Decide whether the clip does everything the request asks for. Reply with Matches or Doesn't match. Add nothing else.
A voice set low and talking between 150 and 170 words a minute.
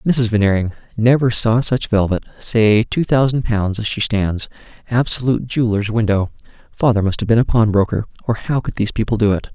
Doesn't match